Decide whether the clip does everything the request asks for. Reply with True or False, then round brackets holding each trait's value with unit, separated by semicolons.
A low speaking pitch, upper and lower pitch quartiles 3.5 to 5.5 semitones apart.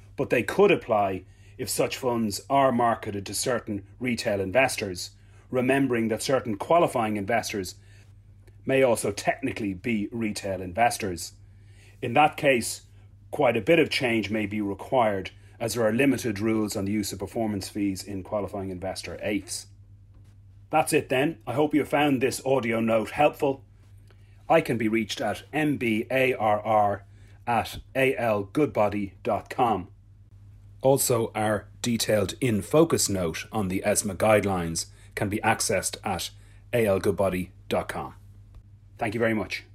False (105 Hz; 2.9 semitones)